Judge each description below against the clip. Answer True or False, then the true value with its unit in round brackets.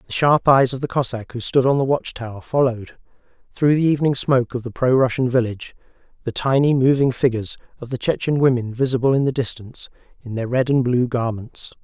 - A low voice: True (125 Hz)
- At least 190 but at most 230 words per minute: True (205 wpm)